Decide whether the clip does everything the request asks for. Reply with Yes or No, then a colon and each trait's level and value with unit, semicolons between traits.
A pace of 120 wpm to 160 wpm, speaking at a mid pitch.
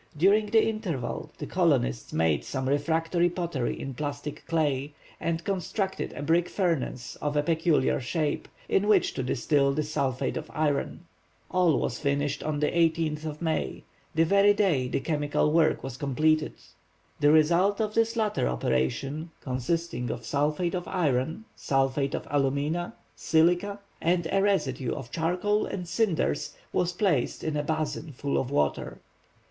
Yes: average, 155 wpm; medium, 155 Hz